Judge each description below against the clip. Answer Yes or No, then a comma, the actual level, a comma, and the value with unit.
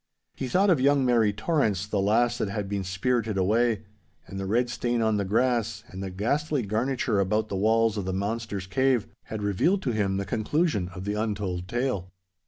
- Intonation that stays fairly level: No, average, 3.6 semitones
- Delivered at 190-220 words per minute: Yes, average, 195 wpm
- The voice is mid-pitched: No, low, 110 Hz